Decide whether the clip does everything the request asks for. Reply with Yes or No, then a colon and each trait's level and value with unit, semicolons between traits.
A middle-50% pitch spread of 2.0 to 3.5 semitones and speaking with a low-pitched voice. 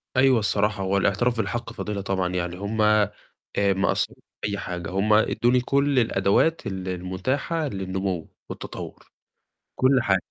No: average, 4.1 semitones; low, 100 Hz